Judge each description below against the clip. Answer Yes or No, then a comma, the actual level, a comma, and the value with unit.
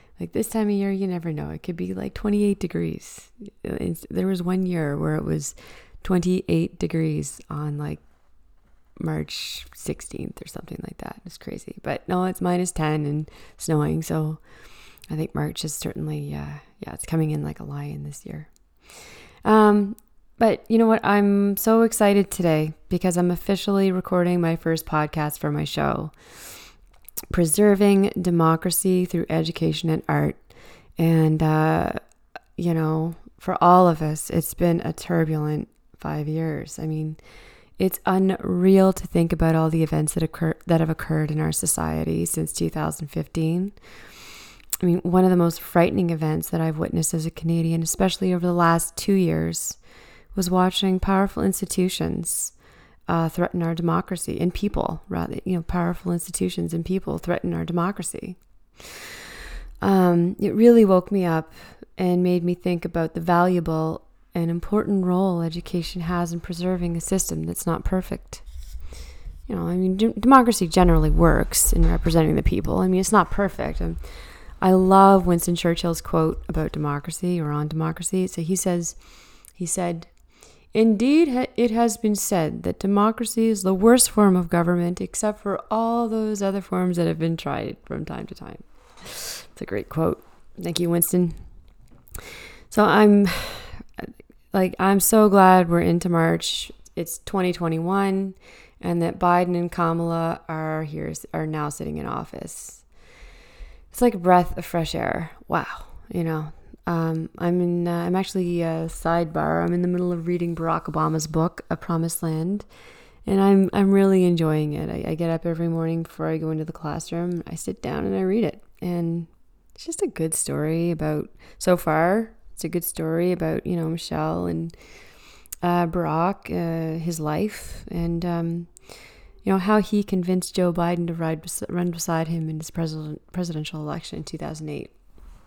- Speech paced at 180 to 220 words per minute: No, average, 165 wpm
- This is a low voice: No, medium, 170 Hz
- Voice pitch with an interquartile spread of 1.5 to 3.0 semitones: Yes, average, 2.7 semitones